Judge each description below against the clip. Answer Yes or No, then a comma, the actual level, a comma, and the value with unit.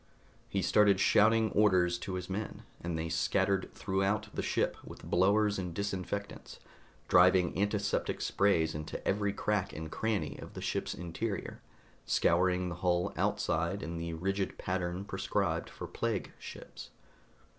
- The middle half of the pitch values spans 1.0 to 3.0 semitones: Yes, narrow, 2.6 semitones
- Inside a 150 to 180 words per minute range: No, average, 140 wpm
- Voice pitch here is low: Yes, very low, 95 Hz